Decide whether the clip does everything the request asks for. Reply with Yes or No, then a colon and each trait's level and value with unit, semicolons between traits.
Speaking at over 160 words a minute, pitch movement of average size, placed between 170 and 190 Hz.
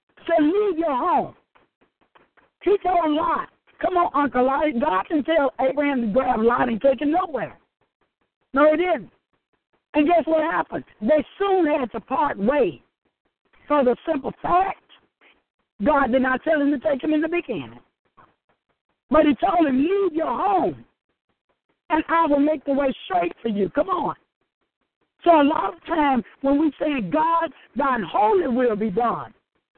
No: average, 170 wpm; average, 3.5 semitones; very high, 305 Hz